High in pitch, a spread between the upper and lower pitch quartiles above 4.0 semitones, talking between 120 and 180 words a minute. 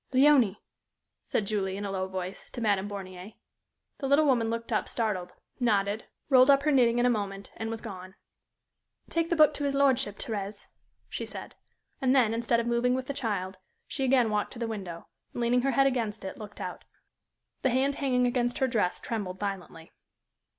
No: high, 230 Hz; average, 4.4 semitones; average, 190 wpm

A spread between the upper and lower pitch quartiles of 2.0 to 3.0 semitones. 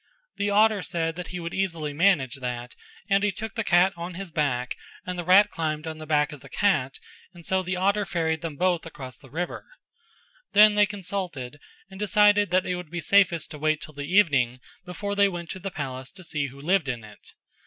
No: average, 4.7 semitones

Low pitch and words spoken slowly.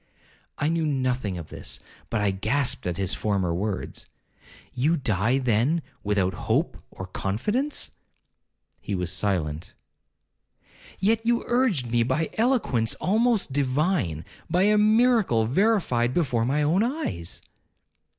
Yes: low, 130 Hz; slow, 125 wpm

